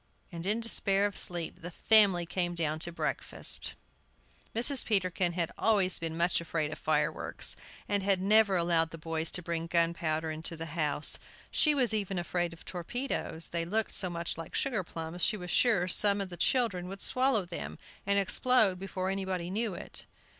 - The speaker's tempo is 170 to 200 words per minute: Yes, average, 180 wpm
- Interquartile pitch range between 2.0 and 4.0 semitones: Yes, average, 3.3 semitones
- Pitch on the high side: No, medium, 180 Hz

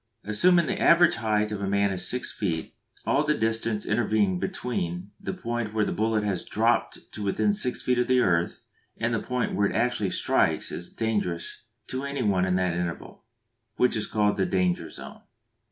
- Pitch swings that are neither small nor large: Yes, average, 4.2 semitones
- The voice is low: Yes, low, 105 Hz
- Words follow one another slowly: No, average, 195 wpm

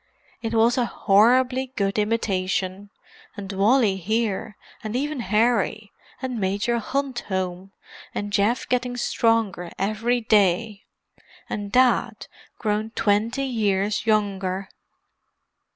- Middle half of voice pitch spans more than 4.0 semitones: No, average, 3.3 semitones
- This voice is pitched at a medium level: No, high, 215 Hz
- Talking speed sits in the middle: No, slow, 105 wpm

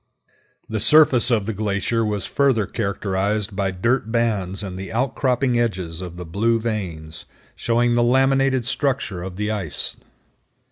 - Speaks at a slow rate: No, average, 145 wpm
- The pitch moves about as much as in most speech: Yes, average, 3.9 semitones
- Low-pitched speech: Yes, low, 110 Hz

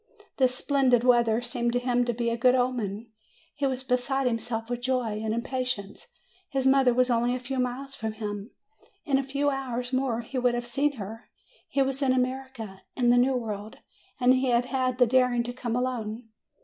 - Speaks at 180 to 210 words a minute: Yes, average, 200 wpm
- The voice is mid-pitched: No, high, 245 Hz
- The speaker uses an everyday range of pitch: No, narrow, 1.8 semitones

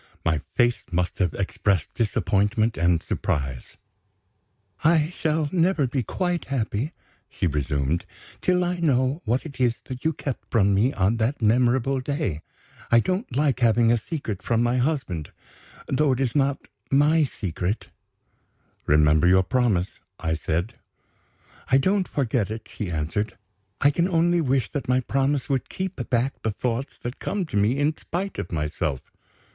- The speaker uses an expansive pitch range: Yes, wide, 6.7 semitones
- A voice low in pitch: Yes, low, 125 Hz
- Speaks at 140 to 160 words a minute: Yes, average, 155 wpm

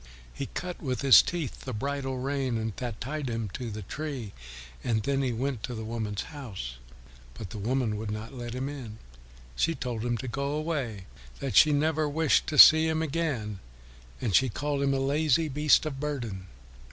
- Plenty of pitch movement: No, average, 4.7 semitones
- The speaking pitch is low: Yes, low, 130 Hz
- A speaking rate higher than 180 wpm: Yes, average, 190 wpm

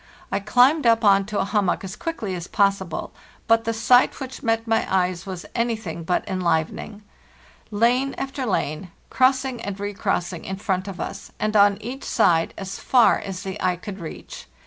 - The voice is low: No, high, 205 Hz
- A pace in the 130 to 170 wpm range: No, average, 190 wpm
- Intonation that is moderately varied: Yes, average, 3.6 semitones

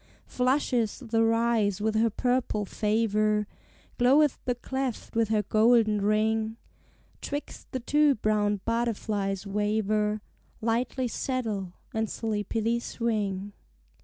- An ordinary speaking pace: No, slow, 105 wpm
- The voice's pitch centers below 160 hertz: No, high, 220 Hz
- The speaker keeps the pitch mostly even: Yes, narrow, 2.2 semitones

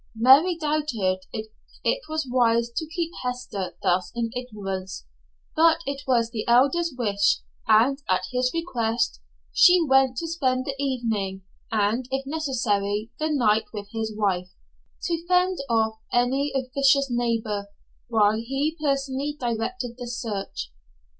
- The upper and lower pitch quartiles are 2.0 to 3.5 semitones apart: No, average, 4.3 semitones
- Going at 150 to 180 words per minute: No, slow, 135 wpm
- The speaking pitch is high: Yes, high, 245 Hz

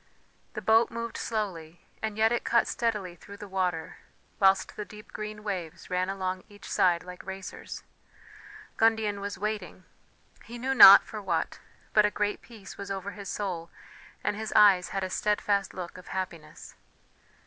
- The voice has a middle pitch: No, high, 200 Hz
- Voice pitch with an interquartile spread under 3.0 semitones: Yes, narrow, 2.4 semitones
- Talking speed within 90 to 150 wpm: No, average, 165 wpm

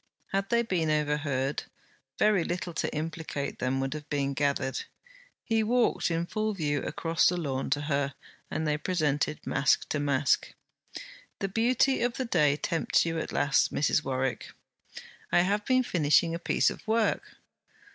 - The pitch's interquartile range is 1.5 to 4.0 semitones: No, average, 5.3 semitones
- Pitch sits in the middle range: Yes, medium, 155 Hz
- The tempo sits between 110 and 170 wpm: Yes, average, 160 wpm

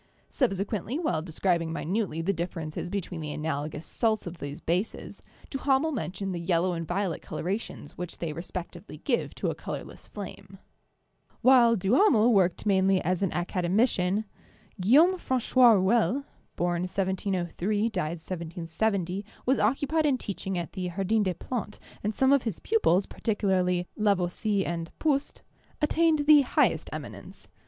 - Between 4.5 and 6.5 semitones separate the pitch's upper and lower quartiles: Yes, average, 4.9 semitones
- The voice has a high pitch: Yes, high, 195 Hz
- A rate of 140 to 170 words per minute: Yes, average, 145 wpm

